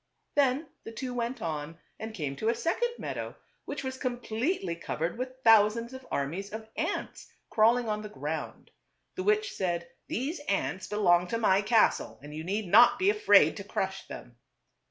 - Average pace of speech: Yes, average, 175 wpm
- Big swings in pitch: Yes, wide, 6.3 semitones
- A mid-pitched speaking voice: No, high, 220 Hz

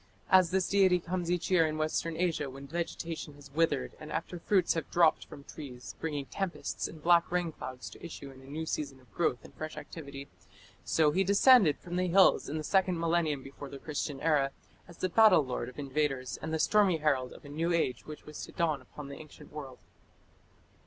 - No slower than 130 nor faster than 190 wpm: No, fast, 205 wpm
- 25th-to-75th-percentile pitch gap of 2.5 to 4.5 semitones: Yes, average, 3.7 semitones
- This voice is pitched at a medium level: Yes, medium, 155 Hz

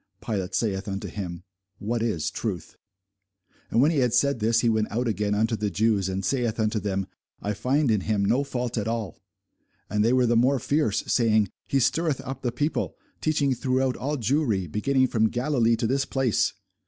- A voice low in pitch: Yes, low, 115 Hz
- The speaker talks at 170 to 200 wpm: Yes, average, 190 wpm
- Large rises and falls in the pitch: No, average, 3.8 semitones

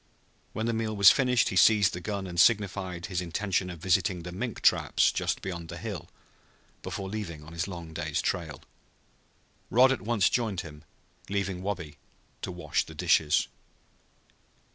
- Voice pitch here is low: Yes, very low, 95 Hz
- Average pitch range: Yes, average, 3.5 semitones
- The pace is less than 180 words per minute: Yes, average, 165 wpm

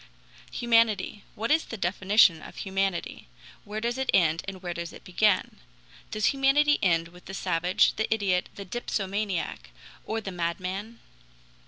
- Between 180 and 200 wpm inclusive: No, average, 150 wpm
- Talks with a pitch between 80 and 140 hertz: No, high, 195 Hz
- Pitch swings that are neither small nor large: Yes, average, 3.7 semitones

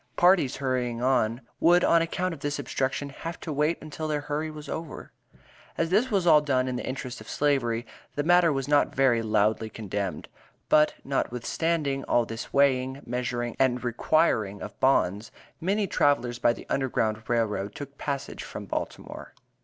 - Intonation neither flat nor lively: Yes, average, 4.3 semitones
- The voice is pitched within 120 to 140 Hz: Yes, low, 135 Hz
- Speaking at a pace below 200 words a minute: Yes, average, 170 wpm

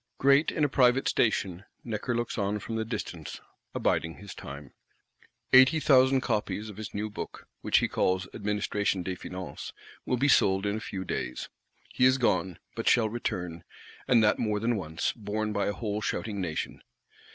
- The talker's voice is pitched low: Yes, low, 105 Hz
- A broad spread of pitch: No, average, 4.2 semitones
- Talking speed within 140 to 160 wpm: No, average, 175 wpm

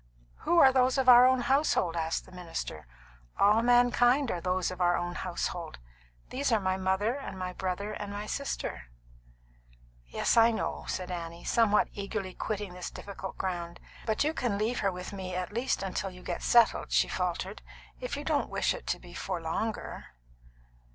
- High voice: Yes, high, 195 Hz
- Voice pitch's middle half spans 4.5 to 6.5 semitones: Yes, average, 4.8 semitones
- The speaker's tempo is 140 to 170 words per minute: No, average, 180 wpm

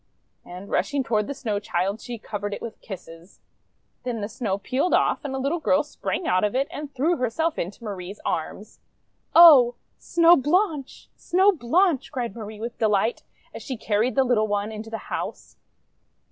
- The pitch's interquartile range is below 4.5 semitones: No, wide, 5.5 semitones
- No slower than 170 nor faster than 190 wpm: Yes, average, 175 wpm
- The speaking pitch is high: Yes, high, 235 Hz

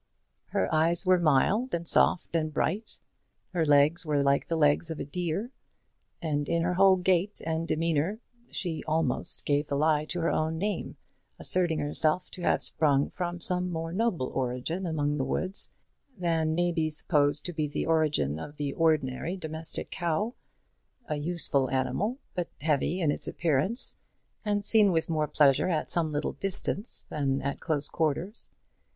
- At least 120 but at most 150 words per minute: No, average, 165 wpm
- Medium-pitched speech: Yes, medium, 160 Hz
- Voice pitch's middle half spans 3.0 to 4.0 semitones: Yes, average, 3.3 semitones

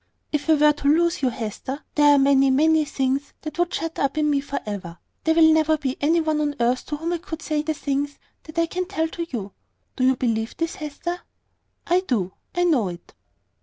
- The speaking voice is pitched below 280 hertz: No, very high, 295 Hz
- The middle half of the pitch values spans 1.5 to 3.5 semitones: Yes, average, 3.2 semitones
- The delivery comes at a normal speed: No, fast, 230 wpm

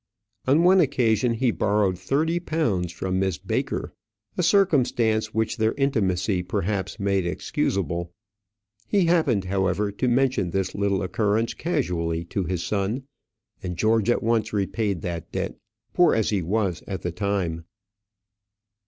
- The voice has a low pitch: Yes, low, 100 Hz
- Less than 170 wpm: Yes, average, 140 wpm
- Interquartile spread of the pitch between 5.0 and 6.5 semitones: No, average, 4.6 semitones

